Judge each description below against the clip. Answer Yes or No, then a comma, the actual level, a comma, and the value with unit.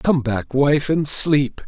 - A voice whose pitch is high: No, medium, 140 Hz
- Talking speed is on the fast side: No, average, 180 wpm